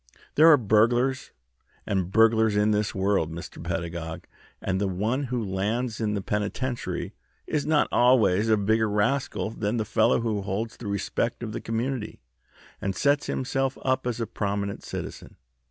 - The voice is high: No, low, 110 Hz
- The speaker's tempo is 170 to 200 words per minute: No, average, 160 wpm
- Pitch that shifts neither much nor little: Yes, average, 3.4 semitones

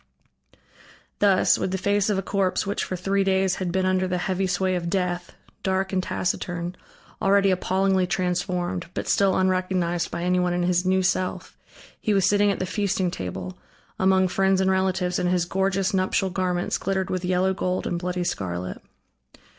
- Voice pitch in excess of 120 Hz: Yes, medium, 185 Hz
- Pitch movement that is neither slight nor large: No, narrow, 1.2 semitones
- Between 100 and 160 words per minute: No, average, 175 wpm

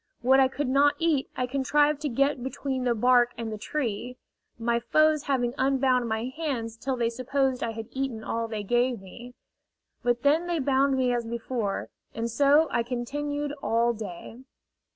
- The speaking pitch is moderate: No, very high, 255 Hz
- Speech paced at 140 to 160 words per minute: No, average, 175 wpm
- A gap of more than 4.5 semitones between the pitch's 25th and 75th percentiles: No, average, 2.9 semitones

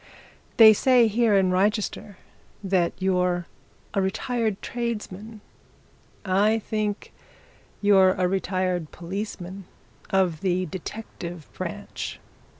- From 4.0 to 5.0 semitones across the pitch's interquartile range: No, average, 2.7 semitones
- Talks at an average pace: No, slow, 95 wpm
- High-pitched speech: Yes, high, 195 Hz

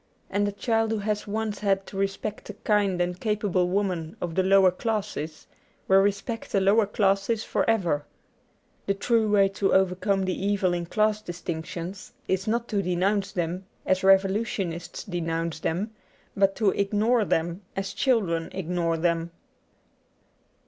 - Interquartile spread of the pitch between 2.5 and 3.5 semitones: Yes, average, 2.9 semitones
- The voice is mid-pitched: No, high, 195 Hz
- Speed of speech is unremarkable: Yes, average, 155 wpm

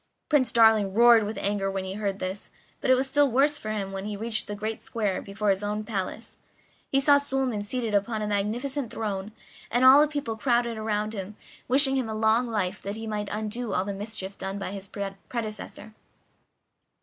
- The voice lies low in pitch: No, high, 215 Hz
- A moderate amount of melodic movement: Yes, average, 3.0 semitones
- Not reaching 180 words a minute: No, average, 195 wpm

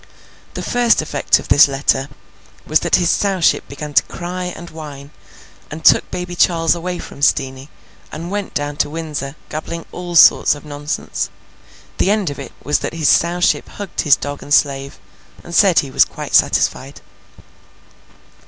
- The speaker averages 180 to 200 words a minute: No, average, 165 wpm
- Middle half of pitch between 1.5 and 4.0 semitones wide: Yes, average, 3.5 semitones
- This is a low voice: No, medium, 155 Hz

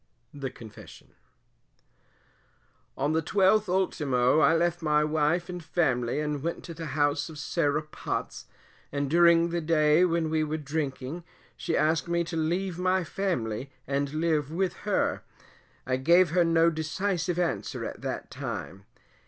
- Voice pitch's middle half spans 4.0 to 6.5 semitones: No, average, 2.8 semitones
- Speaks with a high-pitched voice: No, medium, 160 Hz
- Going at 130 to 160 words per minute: Yes, average, 150 wpm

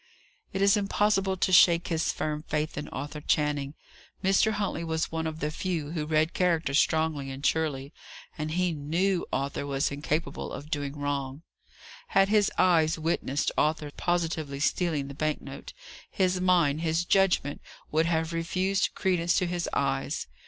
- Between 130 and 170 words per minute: Yes, average, 160 wpm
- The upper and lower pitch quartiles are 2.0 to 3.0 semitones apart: No, average, 3.5 semitones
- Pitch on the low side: No, medium, 160 Hz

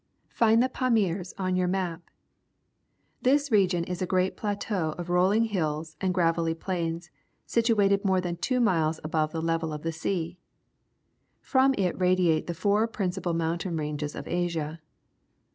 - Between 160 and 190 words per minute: No, average, 150 wpm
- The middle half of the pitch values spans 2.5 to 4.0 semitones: Yes, average, 3.3 semitones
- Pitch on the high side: No, medium, 180 Hz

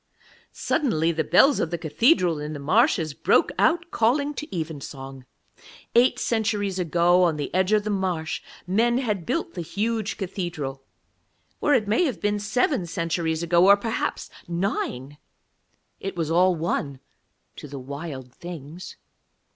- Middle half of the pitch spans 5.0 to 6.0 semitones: Yes, wide, 5.4 semitones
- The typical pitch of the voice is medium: Yes, medium, 180 Hz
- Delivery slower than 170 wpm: Yes, average, 145 wpm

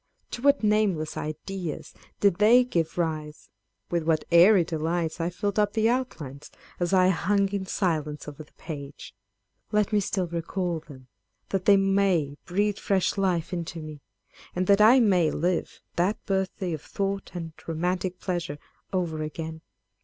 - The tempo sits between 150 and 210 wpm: Yes, average, 160 wpm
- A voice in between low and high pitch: Yes, medium, 180 Hz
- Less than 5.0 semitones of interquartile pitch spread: Yes, average, 3.7 semitones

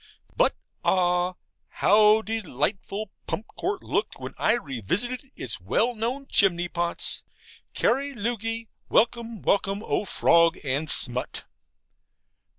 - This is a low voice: No, high, 210 Hz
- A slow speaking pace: Yes, slow, 110 wpm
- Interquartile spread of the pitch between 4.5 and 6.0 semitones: Yes, average, 5.1 semitones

